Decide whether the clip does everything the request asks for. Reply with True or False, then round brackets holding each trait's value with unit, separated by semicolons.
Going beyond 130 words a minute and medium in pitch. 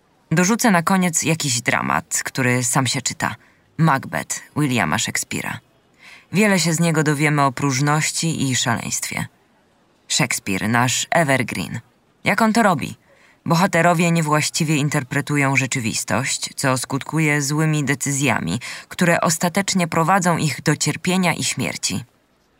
False (115 wpm; 150 Hz)